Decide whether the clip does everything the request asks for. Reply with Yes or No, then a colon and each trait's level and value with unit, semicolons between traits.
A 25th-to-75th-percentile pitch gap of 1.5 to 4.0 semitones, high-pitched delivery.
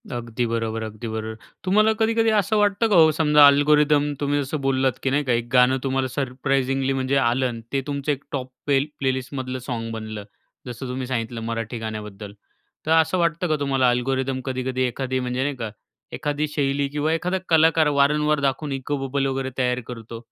No: average, 2.9 semitones; low, 135 Hz